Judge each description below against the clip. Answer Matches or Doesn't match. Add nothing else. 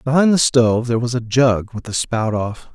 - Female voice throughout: Doesn't match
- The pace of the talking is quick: Matches